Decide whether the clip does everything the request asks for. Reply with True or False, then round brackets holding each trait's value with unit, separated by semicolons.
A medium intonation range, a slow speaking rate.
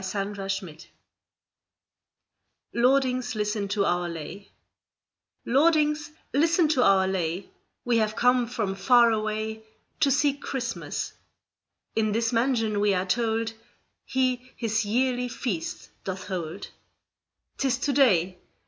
True (4.4 semitones; 115 wpm)